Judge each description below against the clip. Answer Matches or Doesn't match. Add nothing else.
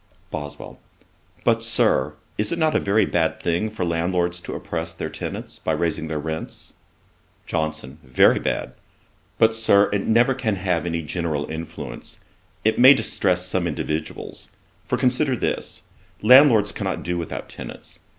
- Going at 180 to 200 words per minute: Doesn't match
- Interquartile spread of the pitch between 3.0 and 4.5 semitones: Doesn't match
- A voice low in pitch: Matches